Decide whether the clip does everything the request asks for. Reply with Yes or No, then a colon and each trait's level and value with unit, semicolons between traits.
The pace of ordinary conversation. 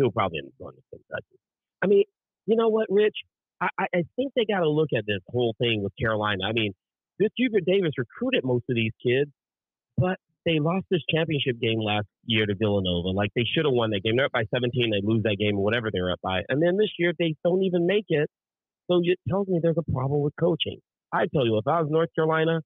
No: fast, 240 wpm